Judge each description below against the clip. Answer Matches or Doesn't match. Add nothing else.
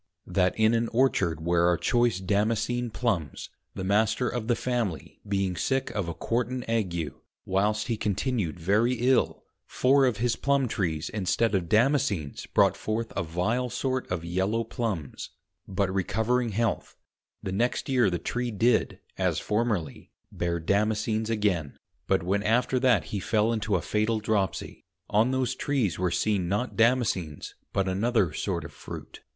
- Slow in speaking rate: Doesn't match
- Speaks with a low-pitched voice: Matches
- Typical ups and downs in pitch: Matches